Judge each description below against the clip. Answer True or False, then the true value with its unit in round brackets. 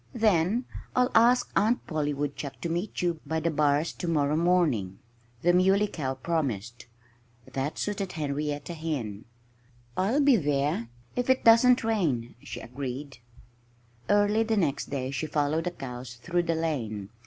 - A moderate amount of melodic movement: False (5.7 semitones)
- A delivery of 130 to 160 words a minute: True (150 wpm)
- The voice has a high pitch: False (155 Hz)